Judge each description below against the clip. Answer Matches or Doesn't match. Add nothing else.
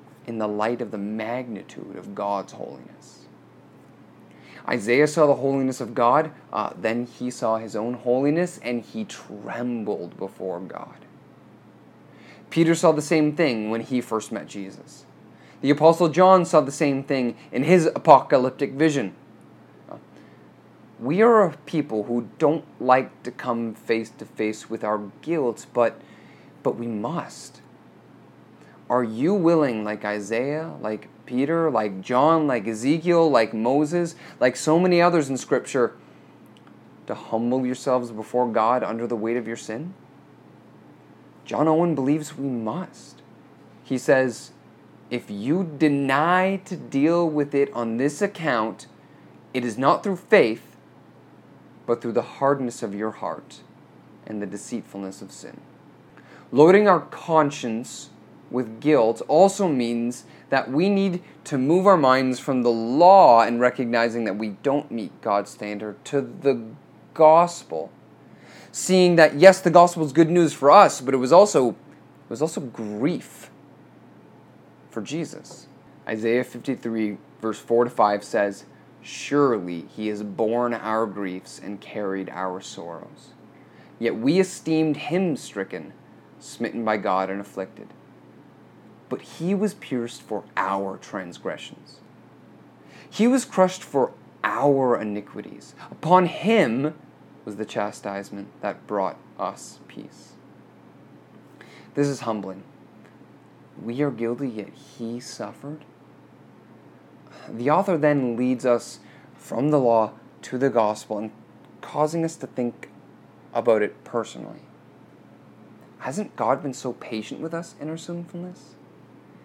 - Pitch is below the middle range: Matches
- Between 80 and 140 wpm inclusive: Matches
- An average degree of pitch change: Doesn't match